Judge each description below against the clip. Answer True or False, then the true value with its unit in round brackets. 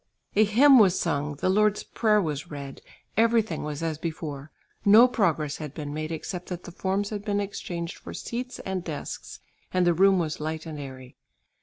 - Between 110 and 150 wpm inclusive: False (185 wpm)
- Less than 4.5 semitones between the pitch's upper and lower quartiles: False (5.1 semitones)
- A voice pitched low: False (175 Hz)